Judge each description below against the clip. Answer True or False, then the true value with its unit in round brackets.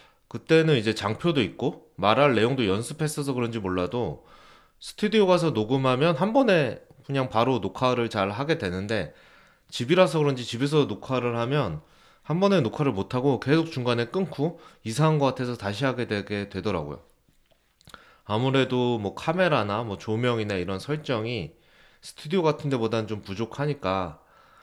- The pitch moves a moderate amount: False (5.7 semitones)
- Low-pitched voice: True (125 Hz)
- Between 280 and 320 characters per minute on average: False (330 characters per minute)